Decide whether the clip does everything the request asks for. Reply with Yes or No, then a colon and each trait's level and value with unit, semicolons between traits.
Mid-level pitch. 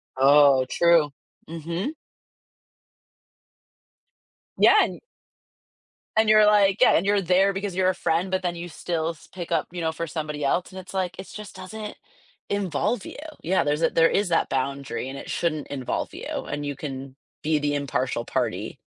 Yes: medium, 170 Hz